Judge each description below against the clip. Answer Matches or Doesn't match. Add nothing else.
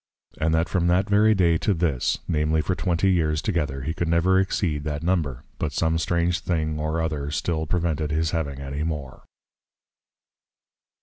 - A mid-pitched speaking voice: Doesn't match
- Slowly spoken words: Doesn't match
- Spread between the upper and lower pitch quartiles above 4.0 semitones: Doesn't match